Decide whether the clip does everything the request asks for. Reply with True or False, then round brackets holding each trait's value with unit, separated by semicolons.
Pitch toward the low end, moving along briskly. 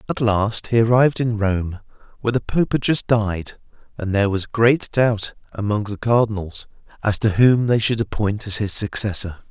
False (110 Hz; 185 wpm)